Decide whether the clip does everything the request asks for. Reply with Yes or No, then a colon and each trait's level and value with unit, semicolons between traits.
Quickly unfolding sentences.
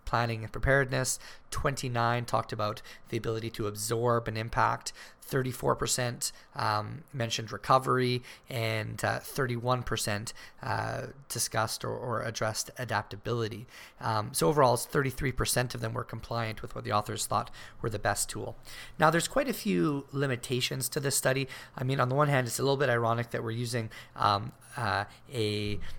No: average, 165 wpm